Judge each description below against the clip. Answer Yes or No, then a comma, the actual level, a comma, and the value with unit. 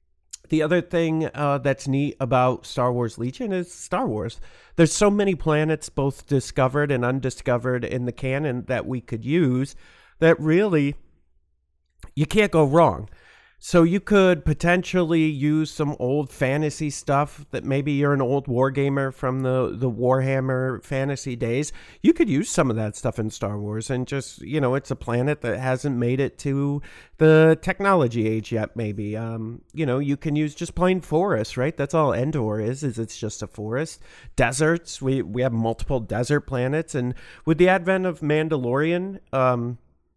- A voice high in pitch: No, low, 135 Hz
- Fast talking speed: No, average, 175 wpm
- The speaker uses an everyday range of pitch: Yes, average, 4.2 semitones